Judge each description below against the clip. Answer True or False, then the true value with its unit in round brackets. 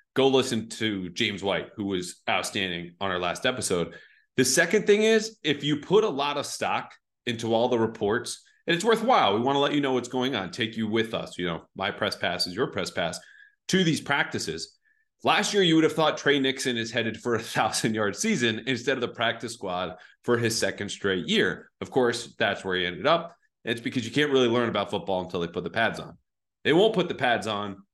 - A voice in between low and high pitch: False (120 Hz)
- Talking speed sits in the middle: False (230 wpm)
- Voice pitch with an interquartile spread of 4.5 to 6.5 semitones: True (5.2 semitones)